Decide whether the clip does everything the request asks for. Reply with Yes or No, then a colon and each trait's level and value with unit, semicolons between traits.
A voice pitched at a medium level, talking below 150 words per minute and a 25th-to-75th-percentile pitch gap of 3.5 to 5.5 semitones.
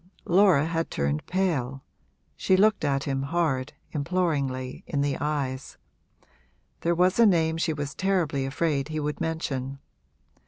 Yes: medium, 150 Hz; slow, 135 wpm; average, 4.0 semitones